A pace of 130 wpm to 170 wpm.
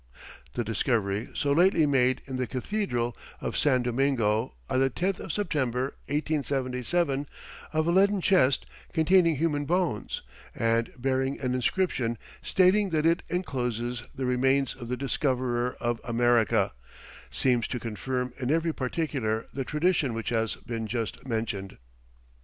Yes: average, 140 wpm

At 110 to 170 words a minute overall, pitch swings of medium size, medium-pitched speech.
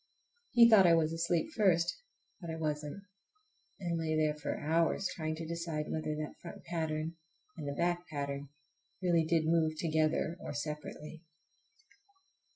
No: average, 145 wpm; narrow, 1.9 semitones; medium, 160 Hz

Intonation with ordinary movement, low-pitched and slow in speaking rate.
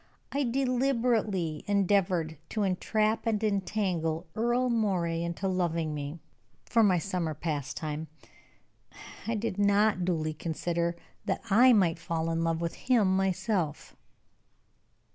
No: average, 4.6 semitones; medium, 185 Hz; slow, 120 wpm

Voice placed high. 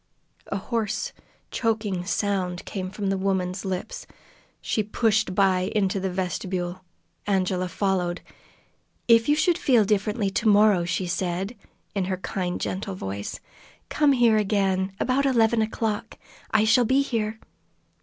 Yes: high, 200 Hz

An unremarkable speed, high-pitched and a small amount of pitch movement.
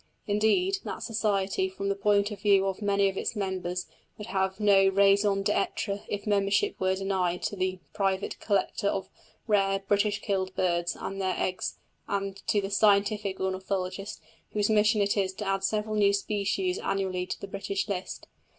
Yes: average, 170 wpm; high, 200 Hz; narrow, 1.4 semitones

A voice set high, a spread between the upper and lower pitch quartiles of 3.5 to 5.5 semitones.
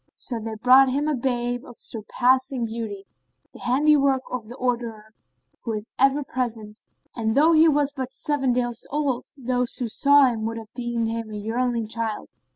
No: high, 245 Hz; average, 2.8 semitones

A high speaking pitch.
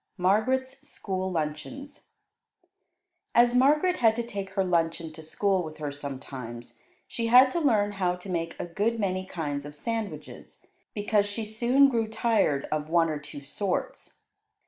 Yes: high, 195 Hz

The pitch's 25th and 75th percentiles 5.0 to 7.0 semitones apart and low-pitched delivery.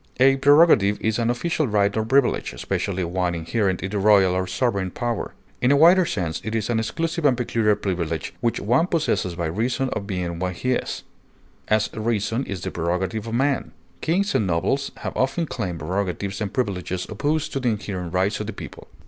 Yes: wide, 5.6 semitones; low, 105 Hz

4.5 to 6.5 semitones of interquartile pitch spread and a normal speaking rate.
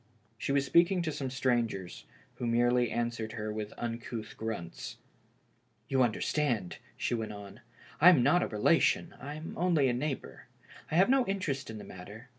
Yes: average, 5.1 semitones; average, 175 wpm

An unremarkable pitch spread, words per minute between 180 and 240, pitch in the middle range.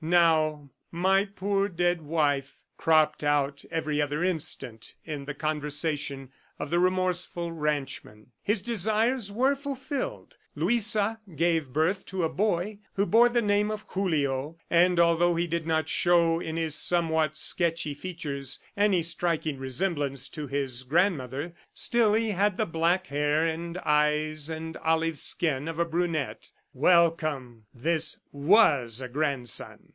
No: average, 3.8 semitones; average, 140 wpm; medium, 165 Hz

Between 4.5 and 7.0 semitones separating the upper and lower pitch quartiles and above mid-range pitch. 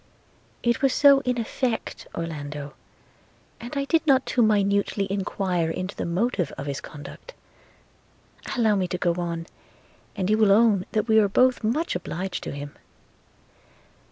Yes: wide, 5.4 semitones; high, 200 Hz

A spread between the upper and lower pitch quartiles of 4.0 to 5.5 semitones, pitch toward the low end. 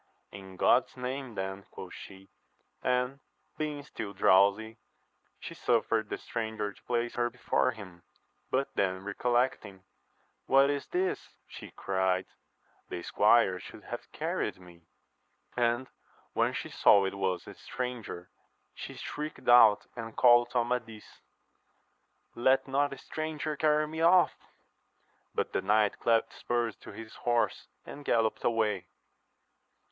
Yes: average, 4.4 semitones; low, 115 Hz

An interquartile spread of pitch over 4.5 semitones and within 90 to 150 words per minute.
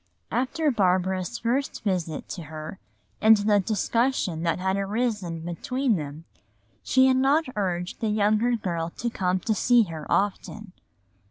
Yes: average, 5.0 semitones; average, 145 wpm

